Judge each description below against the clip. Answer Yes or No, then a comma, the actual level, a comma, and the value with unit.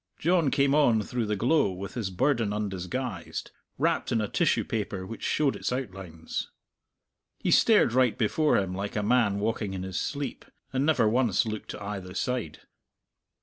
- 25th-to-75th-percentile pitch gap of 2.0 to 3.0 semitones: No, average, 4.8 semitones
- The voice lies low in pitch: Yes, low, 110 Hz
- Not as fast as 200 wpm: Yes, average, 170 wpm